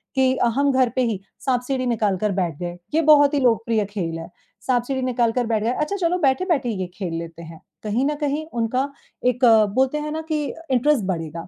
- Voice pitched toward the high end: Yes, high, 245 Hz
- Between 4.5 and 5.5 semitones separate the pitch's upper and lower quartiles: Yes, average, 5.1 semitones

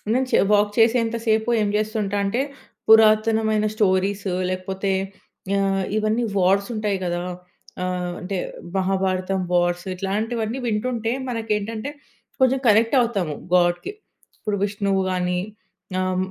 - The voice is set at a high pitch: Yes, high, 205 Hz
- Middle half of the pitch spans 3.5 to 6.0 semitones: No, average, 2.9 semitones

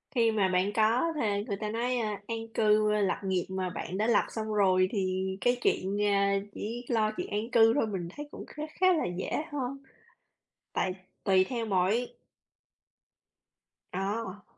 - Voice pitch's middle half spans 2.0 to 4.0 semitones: Yes, average, 3.3 semitones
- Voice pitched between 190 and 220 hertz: Yes, high, 210 Hz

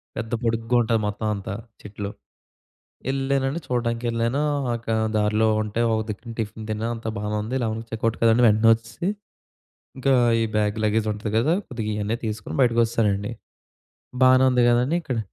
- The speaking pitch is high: No, low, 115 Hz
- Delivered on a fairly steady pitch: Yes, narrow, 2.0 semitones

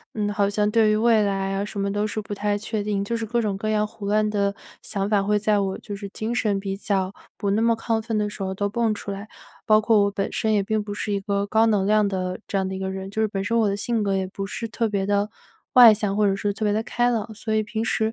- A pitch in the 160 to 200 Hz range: No, high, 210 Hz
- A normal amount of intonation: No, narrow, 1.6 semitones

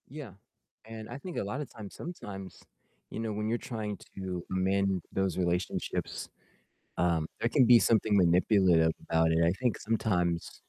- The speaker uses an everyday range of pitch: Yes, average, 4.2 semitones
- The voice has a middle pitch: No, low, 100 Hz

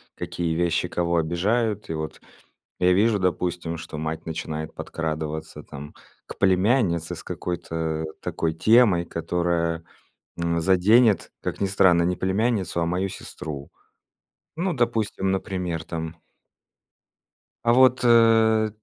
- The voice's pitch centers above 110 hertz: No, very low, 90 Hz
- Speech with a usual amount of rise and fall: Yes, average, 4.3 semitones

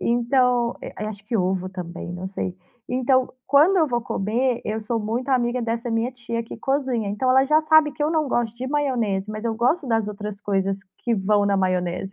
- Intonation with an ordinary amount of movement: Yes, average, 4.2 semitones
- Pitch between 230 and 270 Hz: Yes, high, 235 Hz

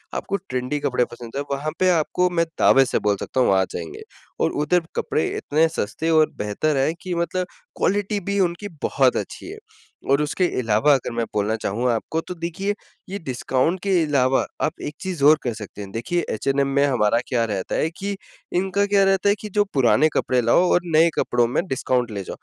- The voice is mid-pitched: Yes, medium, 145 Hz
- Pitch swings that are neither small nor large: No, wide, 6.3 semitones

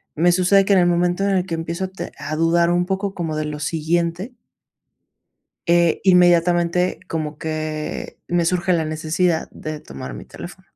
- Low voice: No, medium, 170 Hz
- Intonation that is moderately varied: No, narrow, 2.2 semitones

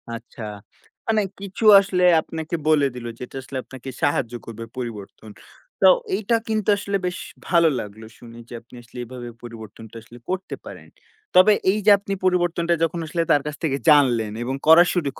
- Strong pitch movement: Yes, wide, 7.3 semitones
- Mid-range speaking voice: Yes, medium, 145 Hz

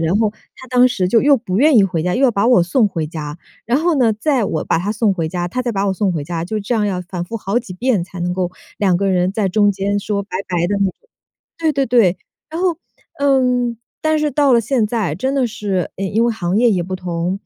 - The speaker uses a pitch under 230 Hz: Yes, high, 205 Hz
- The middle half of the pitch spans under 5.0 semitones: No, average, 5.3 semitones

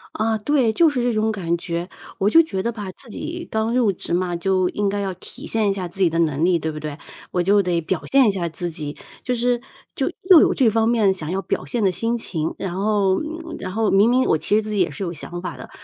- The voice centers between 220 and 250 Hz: No, high, 195 Hz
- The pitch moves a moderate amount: Yes, average, 4.6 semitones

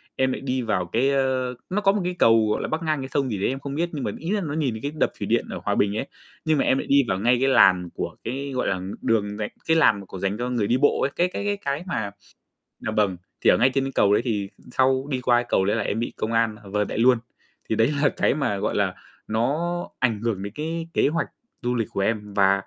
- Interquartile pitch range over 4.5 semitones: Yes, average, 5.1 semitones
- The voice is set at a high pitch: No, low, 125 Hz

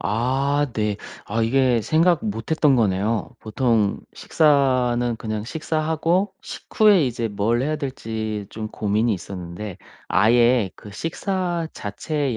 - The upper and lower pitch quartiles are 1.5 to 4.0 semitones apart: No, wide, 5.5 semitones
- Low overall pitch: Yes, low, 120 Hz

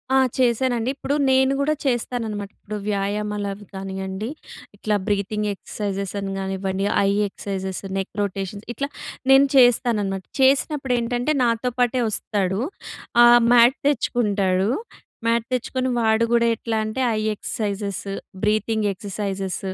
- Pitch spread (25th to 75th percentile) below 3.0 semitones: No, average, 3.6 semitones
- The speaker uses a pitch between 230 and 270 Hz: No, high, 210 Hz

